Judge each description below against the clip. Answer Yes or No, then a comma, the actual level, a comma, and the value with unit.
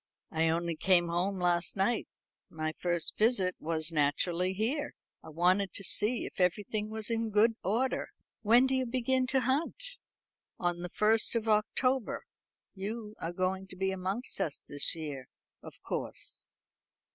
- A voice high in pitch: Yes, high, 195 Hz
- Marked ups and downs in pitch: No, average, 4.8 semitones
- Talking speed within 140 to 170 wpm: Yes, average, 155 wpm